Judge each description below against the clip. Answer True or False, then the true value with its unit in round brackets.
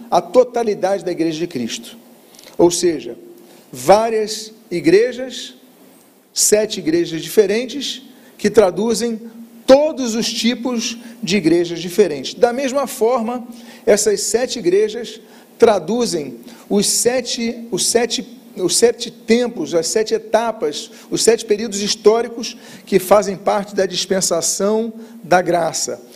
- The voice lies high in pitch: True (225 Hz)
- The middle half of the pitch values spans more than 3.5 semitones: False (3.2 semitones)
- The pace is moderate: False (110 wpm)